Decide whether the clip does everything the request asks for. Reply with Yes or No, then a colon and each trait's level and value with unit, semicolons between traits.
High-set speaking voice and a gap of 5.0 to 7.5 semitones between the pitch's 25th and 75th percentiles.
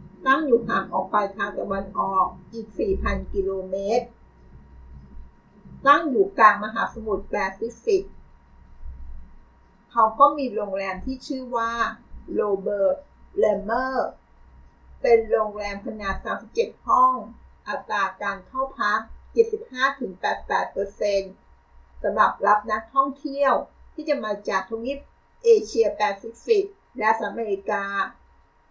Yes: high, 210 Hz; average, 5.3 semitones